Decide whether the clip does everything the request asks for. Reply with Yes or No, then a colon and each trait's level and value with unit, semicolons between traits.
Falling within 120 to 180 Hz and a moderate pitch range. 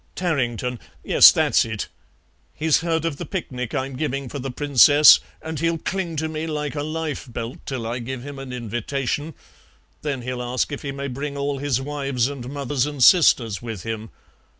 Yes: medium, 140 Hz; average, 3.1 semitones